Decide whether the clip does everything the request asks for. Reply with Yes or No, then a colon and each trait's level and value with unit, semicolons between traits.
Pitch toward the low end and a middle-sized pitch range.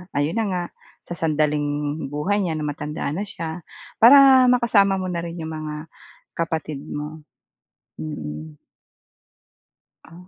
No: medium, 160 Hz; average, 4.0 semitones